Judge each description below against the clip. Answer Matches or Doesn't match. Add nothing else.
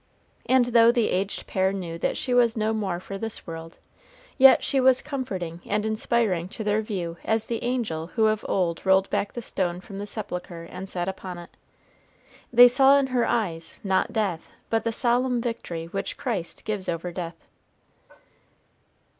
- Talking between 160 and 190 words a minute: Matches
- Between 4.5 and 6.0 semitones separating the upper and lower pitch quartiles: Matches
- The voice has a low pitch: Doesn't match